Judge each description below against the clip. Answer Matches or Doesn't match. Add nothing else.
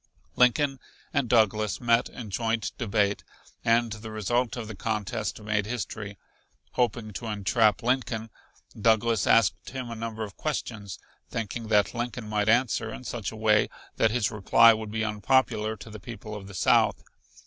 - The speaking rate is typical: Matches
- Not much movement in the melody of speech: Matches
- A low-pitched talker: Matches